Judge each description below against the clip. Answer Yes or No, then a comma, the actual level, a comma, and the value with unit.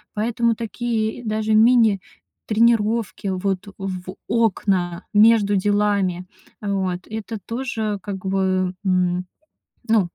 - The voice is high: Yes, high, 205 Hz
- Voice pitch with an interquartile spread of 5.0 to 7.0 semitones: No, average, 2.9 semitones